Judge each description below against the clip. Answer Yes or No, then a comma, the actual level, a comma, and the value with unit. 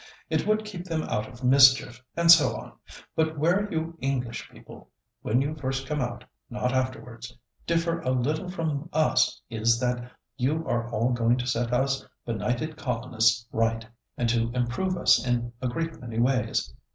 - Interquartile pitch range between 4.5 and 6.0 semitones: Yes, average, 4.8 semitones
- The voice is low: Yes, low, 130 Hz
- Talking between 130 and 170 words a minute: Yes, average, 165 wpm